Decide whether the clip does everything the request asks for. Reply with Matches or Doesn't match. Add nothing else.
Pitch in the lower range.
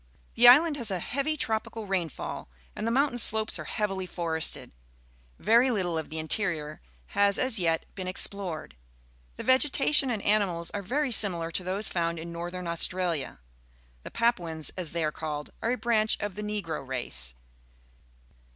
Doesn't match